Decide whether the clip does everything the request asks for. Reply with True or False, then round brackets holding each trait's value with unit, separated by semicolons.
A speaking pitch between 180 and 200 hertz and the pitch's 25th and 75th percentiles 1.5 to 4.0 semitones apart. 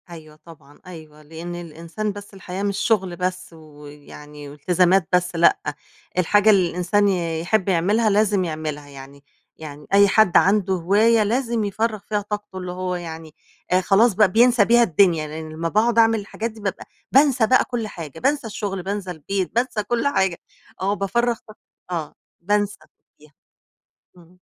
False (190 Hz; 4.4 semitones)